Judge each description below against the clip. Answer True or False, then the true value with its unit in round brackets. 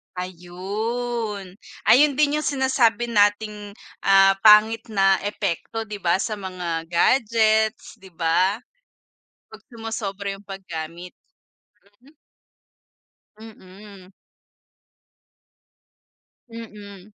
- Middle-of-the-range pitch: False (205 Hz)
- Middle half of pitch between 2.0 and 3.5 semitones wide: True (3.1 semitones)